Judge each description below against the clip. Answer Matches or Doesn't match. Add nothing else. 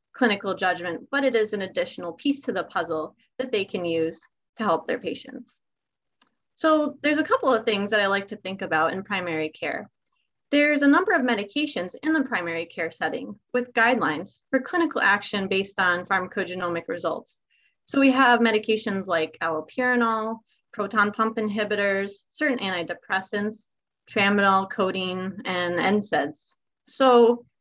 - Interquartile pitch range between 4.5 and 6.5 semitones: Matches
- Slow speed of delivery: Doesn't match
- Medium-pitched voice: Doesn't match